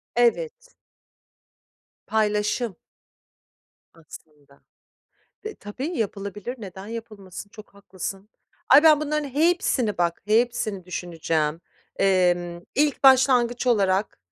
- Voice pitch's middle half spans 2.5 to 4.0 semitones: No, average, 5.2 semitones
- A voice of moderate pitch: No, high, 210 Hz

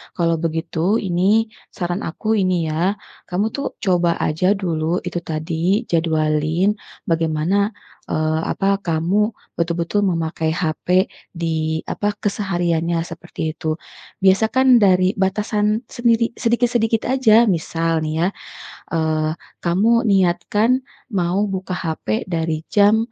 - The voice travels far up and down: No, average, 4.1 semitones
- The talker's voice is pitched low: No, medium, 180 Hz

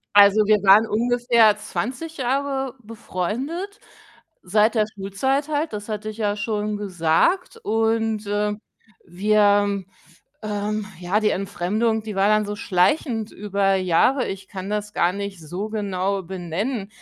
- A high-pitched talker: Yes, high, 210 Hz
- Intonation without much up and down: Yes, narrow, 2.3 semitones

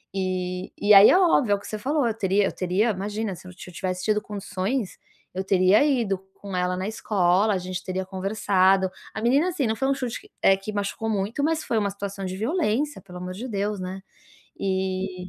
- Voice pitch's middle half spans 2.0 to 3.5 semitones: Yes, average, 2.9 semitones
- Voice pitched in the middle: No, high, 200 Hz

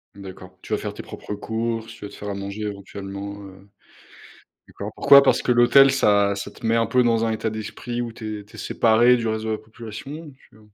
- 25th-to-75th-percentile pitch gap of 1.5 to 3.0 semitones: Yes, average, 2.7 semitones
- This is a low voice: Yes, low, 110 Hz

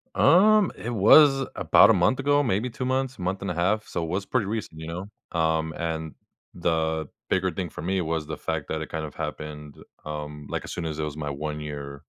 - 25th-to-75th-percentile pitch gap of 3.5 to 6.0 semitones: Yes, wide, 5.6 semitones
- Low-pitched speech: Yes, very low, 85 Hz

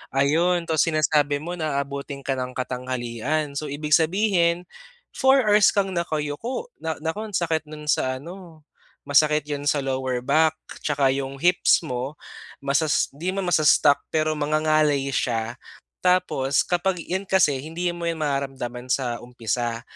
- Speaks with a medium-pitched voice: Yes, medium, 150 Hz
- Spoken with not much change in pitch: No, average, 3.8 semitones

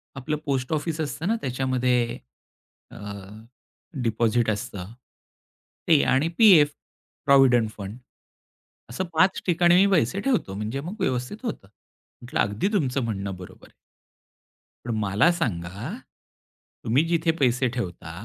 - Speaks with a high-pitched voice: No, low, 130 Hz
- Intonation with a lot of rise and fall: Yes, wide, 6.4 semitones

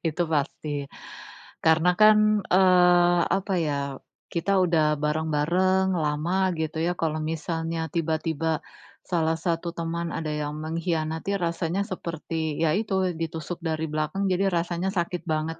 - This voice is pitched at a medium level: Yes, medium, 165 Hz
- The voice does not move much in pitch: Yes, narrow, 2.2 semitones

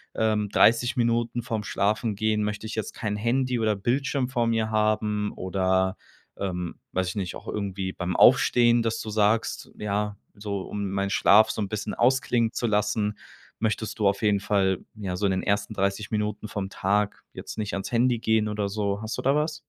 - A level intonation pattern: Yes, narrow, 2.2 semitones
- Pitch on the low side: Yes, low, 105 Hz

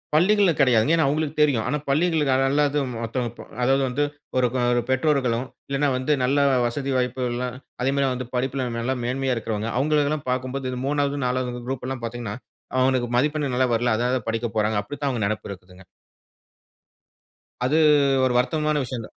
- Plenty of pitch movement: No, average, 2.8 semitones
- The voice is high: No, low, 130 Hz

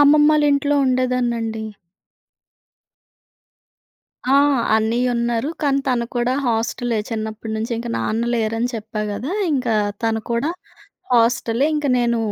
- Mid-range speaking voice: No, high, 235 Hz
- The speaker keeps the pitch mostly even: Yes, narrow, 2.3 semitones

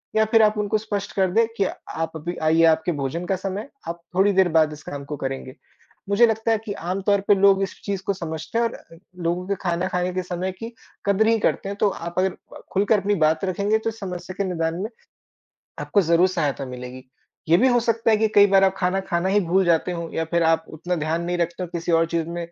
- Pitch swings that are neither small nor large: Yes, average, 3.3 semitones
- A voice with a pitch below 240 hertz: Yes, medium, 185 Hz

